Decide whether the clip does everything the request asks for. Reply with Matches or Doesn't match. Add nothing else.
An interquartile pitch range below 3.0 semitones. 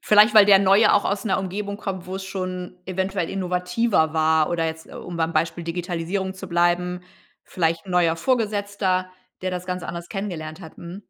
Matches